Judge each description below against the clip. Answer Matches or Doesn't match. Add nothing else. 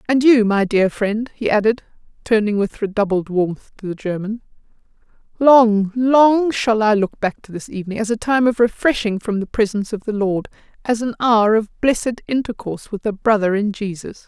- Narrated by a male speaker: Doesn't match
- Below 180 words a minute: Doesn't match